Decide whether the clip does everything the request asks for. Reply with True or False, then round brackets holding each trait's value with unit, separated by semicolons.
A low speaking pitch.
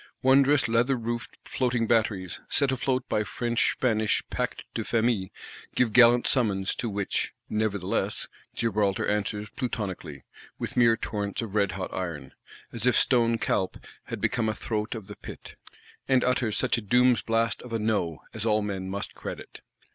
True (110 Hz)